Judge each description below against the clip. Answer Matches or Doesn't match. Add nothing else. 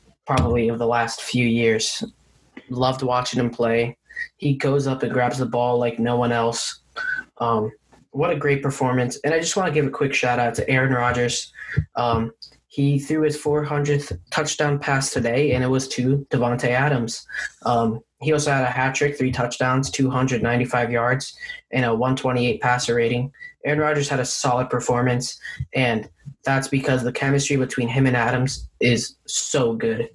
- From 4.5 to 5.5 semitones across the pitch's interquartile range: Doesn't match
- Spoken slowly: Doesn't match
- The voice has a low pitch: Matches